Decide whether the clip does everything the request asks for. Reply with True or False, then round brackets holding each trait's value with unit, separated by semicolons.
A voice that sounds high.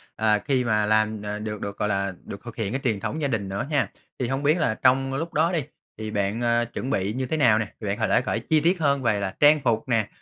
False (115 Hz)